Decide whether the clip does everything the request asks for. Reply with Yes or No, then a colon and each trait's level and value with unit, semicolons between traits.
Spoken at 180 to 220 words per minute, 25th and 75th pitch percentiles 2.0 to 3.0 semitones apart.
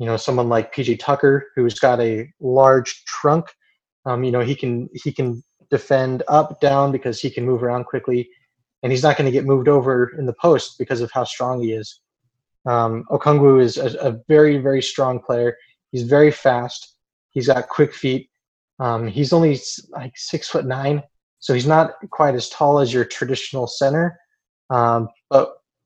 Yes: average, 185 wpm; average, 2.7 semitones